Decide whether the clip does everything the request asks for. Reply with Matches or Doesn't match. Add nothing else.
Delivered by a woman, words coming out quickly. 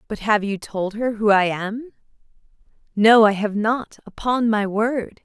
Doesn't match